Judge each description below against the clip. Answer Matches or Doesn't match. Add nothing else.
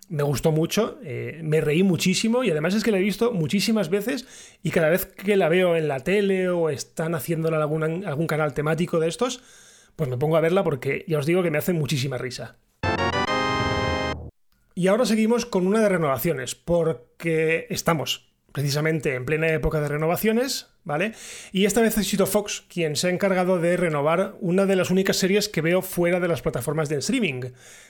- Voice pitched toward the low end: Doesn't match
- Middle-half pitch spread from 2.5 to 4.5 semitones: Matches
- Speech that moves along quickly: Matches